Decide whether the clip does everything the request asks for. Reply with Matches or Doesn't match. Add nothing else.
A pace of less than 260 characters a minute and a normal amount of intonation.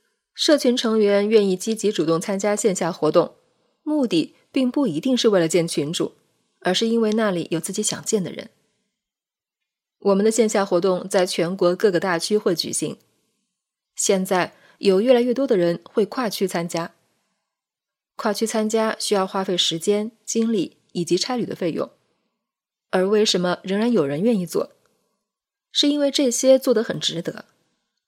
Matches